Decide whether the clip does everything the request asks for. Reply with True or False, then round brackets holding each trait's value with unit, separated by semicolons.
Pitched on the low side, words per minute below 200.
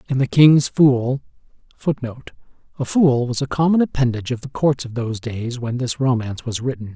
True (130 Hz; 190 wpm)